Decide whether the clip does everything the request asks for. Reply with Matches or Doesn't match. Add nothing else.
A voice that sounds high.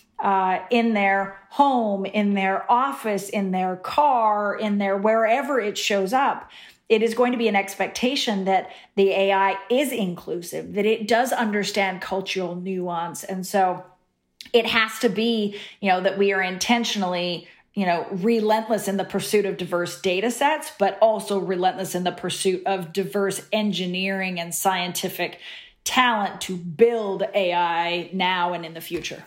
Matches